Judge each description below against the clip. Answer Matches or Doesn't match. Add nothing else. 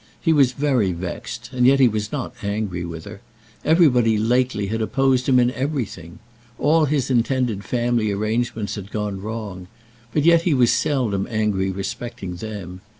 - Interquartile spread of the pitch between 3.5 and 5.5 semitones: Matches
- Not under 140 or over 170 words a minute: Matches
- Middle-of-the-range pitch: Doesn't match